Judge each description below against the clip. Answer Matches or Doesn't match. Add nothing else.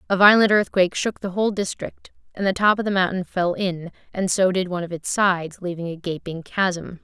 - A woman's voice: Matches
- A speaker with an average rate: Doesn't match